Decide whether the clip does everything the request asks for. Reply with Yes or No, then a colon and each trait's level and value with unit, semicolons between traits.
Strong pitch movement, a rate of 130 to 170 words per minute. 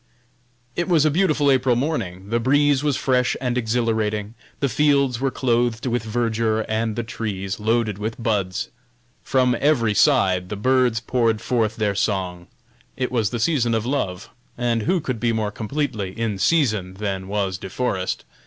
No: average, 3.5 semitones; average, 165 wpm